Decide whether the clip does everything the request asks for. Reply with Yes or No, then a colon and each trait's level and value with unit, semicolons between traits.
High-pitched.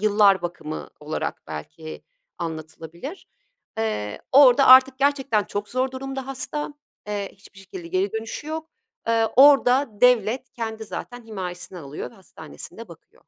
Yes: high, 220 Hz